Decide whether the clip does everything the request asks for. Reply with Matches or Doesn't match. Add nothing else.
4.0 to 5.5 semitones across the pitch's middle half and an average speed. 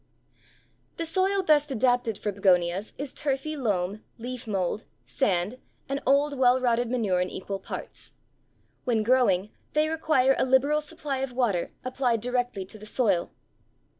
Matches